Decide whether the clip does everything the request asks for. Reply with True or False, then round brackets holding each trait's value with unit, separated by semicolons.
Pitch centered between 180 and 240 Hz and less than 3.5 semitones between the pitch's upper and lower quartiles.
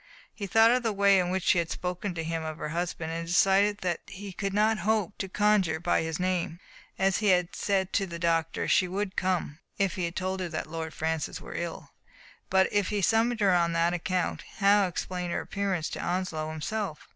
True (185 Hz; 3.0 semitones)